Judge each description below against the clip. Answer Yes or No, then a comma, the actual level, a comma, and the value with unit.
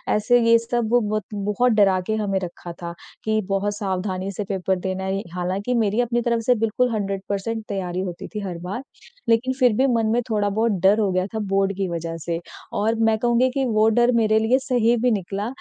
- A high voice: Yes, high, 210 Hz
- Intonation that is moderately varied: Yes, average, 3.1 semitones